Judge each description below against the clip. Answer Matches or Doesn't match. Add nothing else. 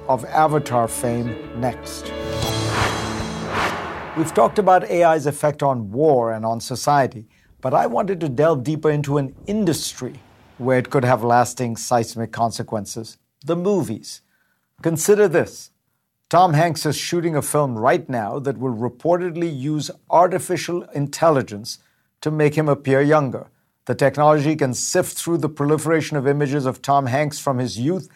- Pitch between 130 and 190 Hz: Matches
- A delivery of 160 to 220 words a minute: Doesn't match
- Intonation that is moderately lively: Matches